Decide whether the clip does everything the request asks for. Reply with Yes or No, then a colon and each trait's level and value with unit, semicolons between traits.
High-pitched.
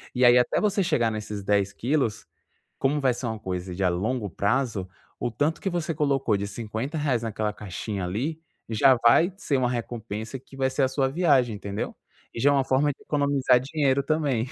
No: low, 125 Hz